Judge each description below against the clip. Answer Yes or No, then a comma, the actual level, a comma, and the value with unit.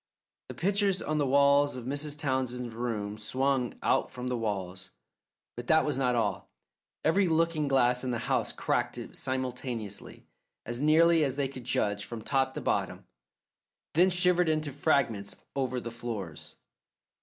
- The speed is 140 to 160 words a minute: Yes, average, 155 wpm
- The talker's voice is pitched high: No, low, 130 Hz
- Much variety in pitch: No, average, 4.1 semitones